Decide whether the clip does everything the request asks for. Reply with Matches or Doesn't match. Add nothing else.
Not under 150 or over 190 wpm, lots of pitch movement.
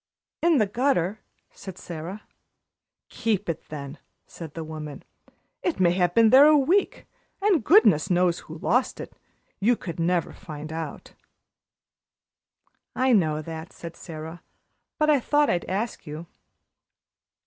Doesn't match